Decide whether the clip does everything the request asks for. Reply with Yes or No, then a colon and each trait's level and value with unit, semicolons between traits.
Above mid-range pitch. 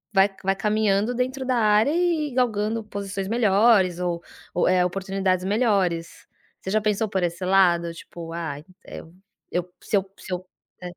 Yes: high, 195 Hz